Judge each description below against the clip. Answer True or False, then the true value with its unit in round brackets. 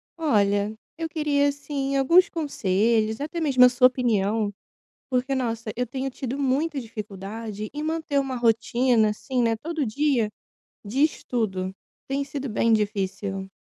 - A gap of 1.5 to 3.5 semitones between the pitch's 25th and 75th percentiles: False (4.7 semitones)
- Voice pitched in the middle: False (250 Hz)